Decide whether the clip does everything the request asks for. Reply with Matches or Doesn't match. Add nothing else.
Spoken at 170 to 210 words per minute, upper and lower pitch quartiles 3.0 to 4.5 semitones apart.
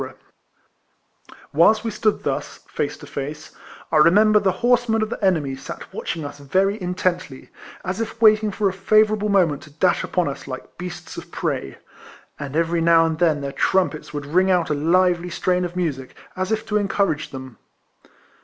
Doesn't match